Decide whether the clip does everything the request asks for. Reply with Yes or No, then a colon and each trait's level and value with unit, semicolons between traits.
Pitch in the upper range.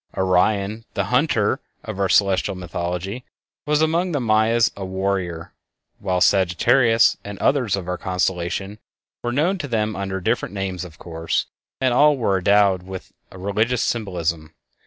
No: low, 100 Hz